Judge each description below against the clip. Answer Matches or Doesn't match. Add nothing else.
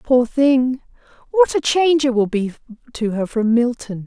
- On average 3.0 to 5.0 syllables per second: Matches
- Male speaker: Doesn't match